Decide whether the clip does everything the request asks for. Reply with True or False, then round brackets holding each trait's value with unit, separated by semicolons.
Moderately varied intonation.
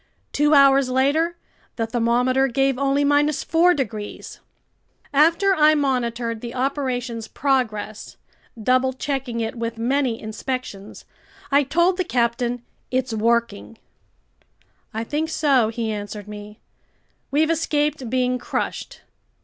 True (3.6 semitones)